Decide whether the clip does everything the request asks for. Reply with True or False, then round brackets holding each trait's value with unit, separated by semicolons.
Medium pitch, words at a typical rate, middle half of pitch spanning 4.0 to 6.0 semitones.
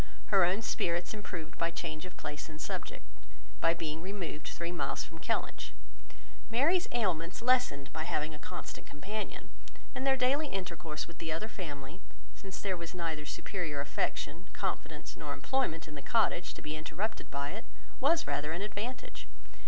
True (175 Hz; 165 wpm; 5.4 semitones)